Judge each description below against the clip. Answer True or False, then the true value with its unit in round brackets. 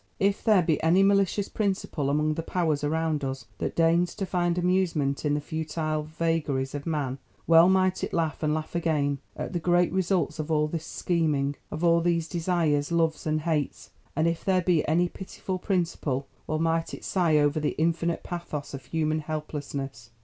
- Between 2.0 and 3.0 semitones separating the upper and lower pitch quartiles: True (2.6 semitones)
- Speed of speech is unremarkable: True (185 wpm)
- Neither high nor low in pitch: True (160 Hz)